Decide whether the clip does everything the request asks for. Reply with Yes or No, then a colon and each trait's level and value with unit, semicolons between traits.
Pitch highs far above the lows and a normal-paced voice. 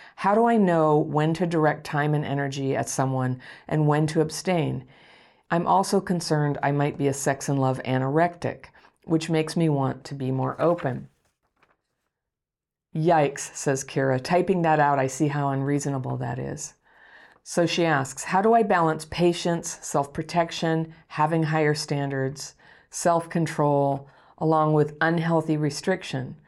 No: average, 3.0 semitones; average, 150 wpm